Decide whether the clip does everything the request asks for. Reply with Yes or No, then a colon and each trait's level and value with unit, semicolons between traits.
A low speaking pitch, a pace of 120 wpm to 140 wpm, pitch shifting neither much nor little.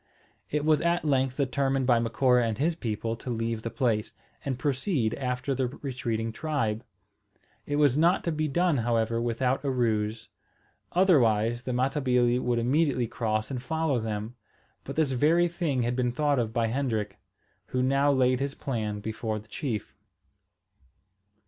No: low, 125 Hz; average, 160 wpm; average, 3.7 semitones